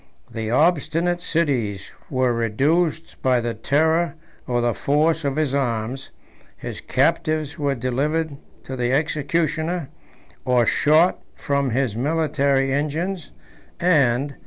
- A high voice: No, medium, 140 Hz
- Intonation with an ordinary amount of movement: Yes, average, 4.0 semitones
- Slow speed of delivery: Yes, slow, 115 wpm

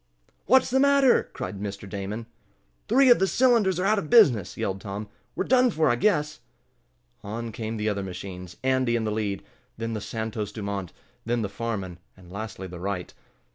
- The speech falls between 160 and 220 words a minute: Yes, average, 180 wpm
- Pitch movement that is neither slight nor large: No, wide, 8.0 semitones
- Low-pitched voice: Yes, low, 110 Hz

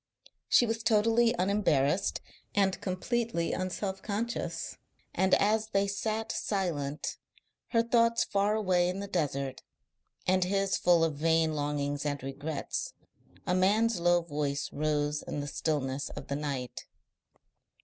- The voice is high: No, medium, 180 Hz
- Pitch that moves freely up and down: Yes, wide, 6.0 semitones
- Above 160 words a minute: No, slow, 135 wpm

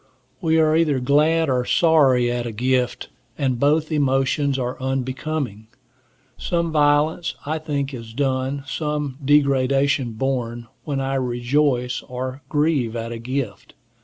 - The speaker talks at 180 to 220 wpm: No, slow, 135 wpm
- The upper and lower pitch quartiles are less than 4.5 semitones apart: Yes, average, 2.9 semitones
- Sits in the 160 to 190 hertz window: No, low, 135 Hz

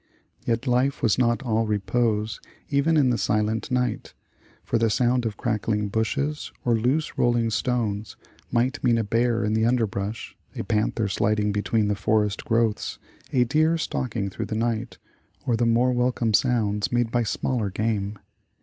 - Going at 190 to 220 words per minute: No, average, 160 wpm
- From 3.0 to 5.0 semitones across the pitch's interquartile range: No, narrow, 2.5 semitones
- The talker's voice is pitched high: No, low, 115 Hz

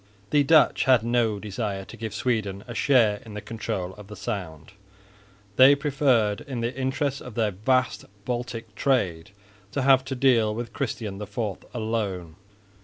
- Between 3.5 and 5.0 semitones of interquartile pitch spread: Yes, average, 4.0 semitones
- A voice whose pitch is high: No, low, 115 Hz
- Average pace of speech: Yes, average, 160 wpm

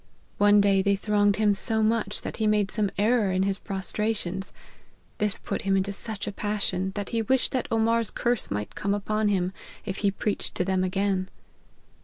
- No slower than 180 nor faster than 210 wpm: Yes, average, 195 wpm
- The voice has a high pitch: Yes, high, 205 Hz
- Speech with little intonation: Yes, narrow, 1.9 semitones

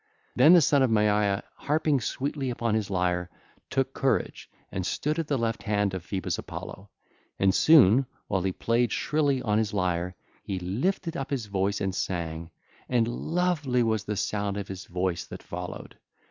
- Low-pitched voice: Yes, low, 105 Hz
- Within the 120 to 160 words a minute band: No, average, 175 wpm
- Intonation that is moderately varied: No, wide, 6.0 semitones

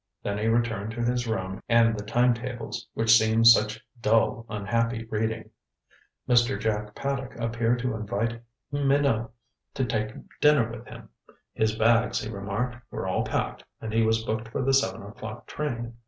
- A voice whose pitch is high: No, low, 115 Hz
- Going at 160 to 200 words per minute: Yes, average, 165 wpm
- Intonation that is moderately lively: No, narrow, 1.7 semitones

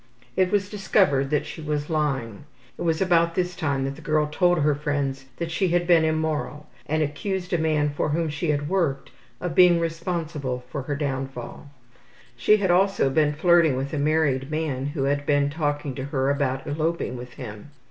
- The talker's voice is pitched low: No, medium, 150 Hz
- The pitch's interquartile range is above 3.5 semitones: No, average, 3.2 semitones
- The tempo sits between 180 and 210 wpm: Yes, average, 190 wpm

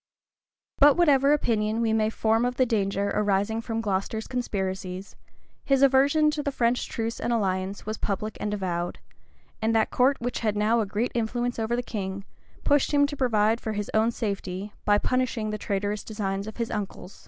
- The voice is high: Yes, high, 220 Hz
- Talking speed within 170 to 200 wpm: Yes, average, 185 wpm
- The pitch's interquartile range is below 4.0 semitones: Yes, average, 3.2 semitones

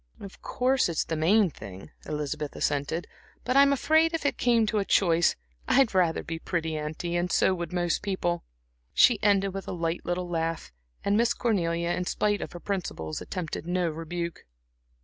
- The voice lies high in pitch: No, medium, 175 Hz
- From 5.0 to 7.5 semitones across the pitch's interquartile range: No, average, 3.9 semitones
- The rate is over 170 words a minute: Yes, average, 180 wpm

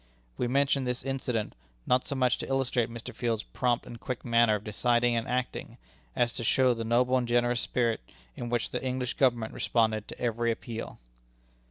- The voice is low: Yes, low, 120 Hz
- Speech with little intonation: Yes, narrow, 1.5 semitones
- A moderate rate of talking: Yes, average, 190 wpm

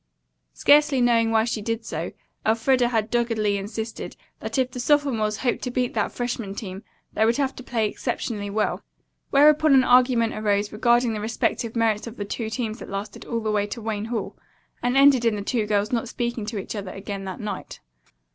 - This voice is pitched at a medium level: No, high, 225 Hz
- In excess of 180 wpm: Yes, average, 200 wpm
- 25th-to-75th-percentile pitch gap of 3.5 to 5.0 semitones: No, narrow, 2.6 semitones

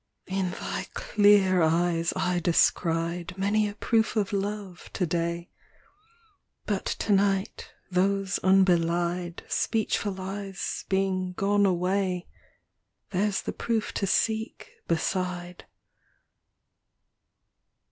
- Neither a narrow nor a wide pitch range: No, narrow, 2.3 semitones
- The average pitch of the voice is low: No, high, 190 Hz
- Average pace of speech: No, slow, 100 wpm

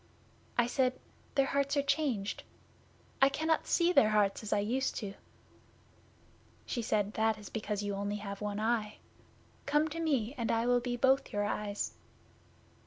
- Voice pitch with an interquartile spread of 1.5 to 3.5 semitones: No, average, 4.7 semitones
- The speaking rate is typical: Yes, average, 165 wpm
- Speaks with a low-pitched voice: No, high, 230 Hz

